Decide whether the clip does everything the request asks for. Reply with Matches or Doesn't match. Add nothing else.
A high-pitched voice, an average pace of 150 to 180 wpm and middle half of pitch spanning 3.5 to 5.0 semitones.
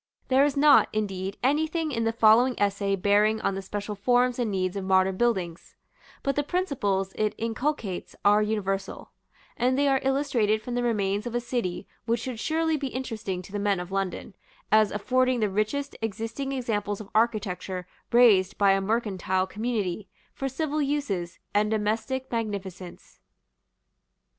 Matches